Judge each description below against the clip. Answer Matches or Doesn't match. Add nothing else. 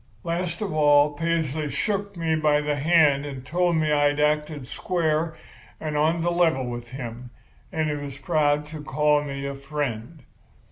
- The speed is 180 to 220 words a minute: Doesn't match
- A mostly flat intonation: Matches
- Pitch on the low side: Doesn't match